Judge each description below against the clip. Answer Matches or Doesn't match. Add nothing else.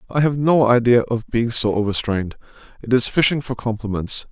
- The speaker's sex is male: Matches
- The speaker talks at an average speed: Matches